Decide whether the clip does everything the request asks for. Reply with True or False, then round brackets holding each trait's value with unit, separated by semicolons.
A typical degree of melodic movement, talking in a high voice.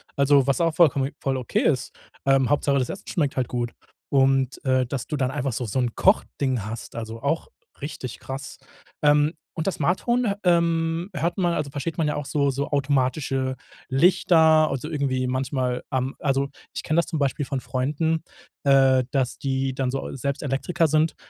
False (3.2 semitones; 140 Hz)